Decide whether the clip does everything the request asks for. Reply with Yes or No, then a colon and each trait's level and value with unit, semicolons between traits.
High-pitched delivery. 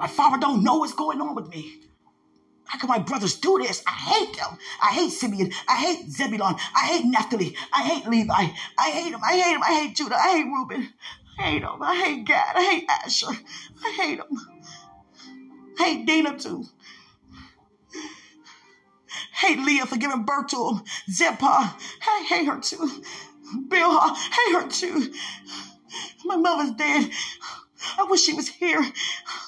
Yes: very high, 305 Hz